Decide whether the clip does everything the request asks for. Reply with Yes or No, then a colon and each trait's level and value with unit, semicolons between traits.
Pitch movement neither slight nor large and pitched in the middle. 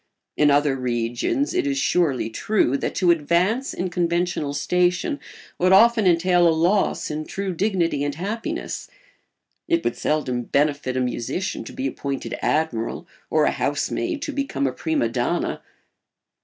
No: wide, 5.7 semitones; medium, 170 Hz